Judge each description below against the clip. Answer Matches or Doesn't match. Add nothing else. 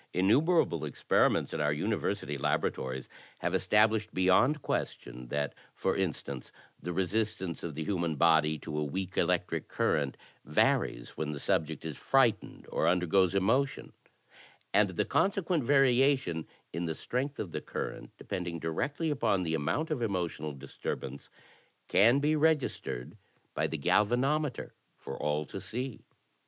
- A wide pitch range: Matches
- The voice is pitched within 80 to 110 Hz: Matches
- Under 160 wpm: Matches